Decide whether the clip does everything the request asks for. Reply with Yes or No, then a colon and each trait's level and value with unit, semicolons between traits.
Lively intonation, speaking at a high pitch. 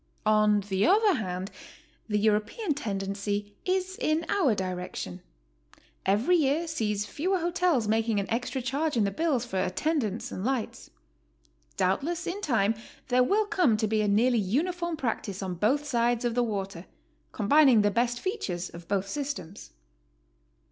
Yes: wide, 7.1 semitones; high, 230 Hz